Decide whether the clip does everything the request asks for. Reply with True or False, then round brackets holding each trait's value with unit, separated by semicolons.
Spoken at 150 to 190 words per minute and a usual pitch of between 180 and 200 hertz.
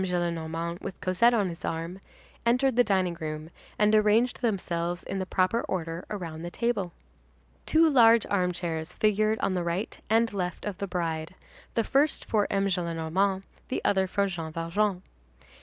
True (160 wpm; 185 Hz)